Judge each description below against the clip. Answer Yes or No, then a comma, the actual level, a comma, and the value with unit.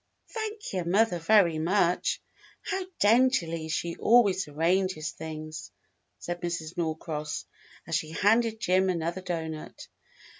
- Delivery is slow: Yes, slow, 115 wpm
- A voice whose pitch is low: No, medium, 175 Hz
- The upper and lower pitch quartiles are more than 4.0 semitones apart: Yes, average, 4.4 semitones